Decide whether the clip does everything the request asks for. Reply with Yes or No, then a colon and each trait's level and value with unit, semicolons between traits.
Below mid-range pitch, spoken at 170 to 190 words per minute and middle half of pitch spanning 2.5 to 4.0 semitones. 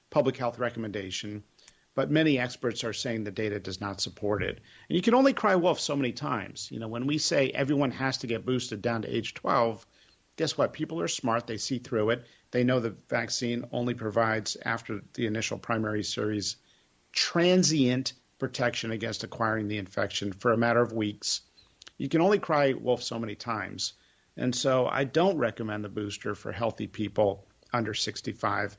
Yes: low, 115 Hz; average, 185 wpm; average, 3.6 semitones